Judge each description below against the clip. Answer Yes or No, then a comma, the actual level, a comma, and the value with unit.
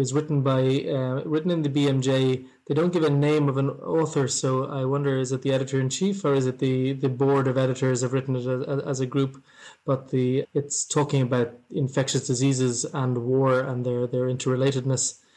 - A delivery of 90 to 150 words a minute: No, fast, 205 wpm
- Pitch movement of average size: No, narrow, 1.4 semitones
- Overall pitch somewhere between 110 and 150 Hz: Yes, low, 135 Hz